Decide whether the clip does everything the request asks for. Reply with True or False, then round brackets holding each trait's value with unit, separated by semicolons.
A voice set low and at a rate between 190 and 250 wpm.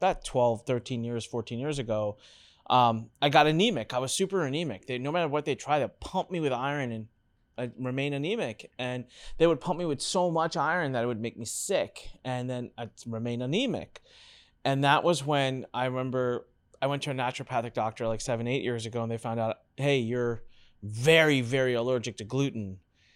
True (125 Hz; 200 wpm)